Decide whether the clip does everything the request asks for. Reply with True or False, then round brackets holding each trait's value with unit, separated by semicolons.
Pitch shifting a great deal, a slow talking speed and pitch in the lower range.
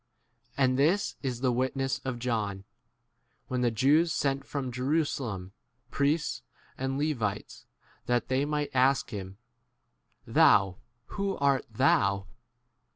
False (3.3 semitones; 120 wpm; 130 Hz)